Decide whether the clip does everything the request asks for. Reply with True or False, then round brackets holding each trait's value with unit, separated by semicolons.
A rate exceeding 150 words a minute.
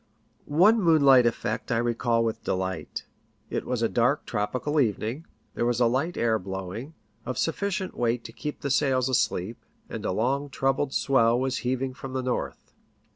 True (170 wpm)